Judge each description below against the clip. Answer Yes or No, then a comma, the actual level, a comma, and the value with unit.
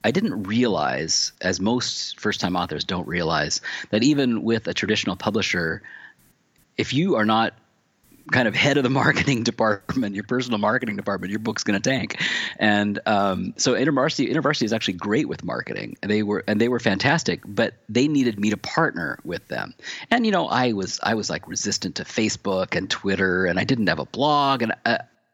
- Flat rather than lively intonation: No, average, 4.1 semitones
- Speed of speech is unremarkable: Yes, average, 190 wpm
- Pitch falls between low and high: No, low, 110 Hz